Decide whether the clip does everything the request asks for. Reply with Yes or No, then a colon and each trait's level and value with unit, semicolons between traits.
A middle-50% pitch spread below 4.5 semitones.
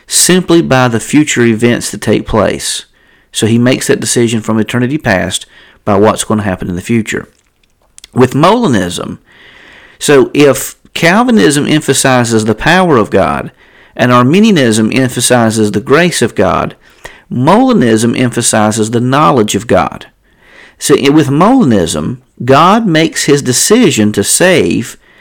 No: average, 4.9 semitones